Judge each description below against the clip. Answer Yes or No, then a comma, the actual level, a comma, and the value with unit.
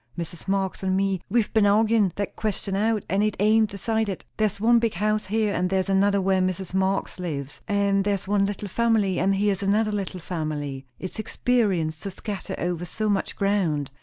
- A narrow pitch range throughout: Yes, narrow, 2.3 semitones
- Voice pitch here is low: No, high, 195 Hz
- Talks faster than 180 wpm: Yes, average, 190 wpm